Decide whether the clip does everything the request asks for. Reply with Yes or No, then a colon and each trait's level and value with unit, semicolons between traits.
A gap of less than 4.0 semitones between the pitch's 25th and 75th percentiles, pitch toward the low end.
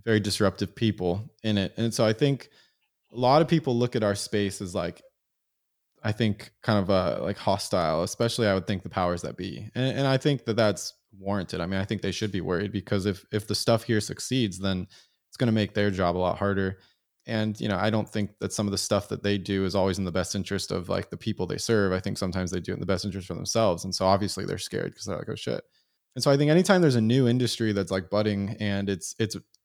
Yes: average, 2.8 semitones; low, 105 Hz